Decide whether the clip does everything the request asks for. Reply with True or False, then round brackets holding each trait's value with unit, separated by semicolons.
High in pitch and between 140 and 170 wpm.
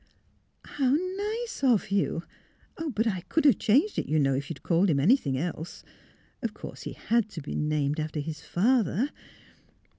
False (200 Hz; 185 wpm)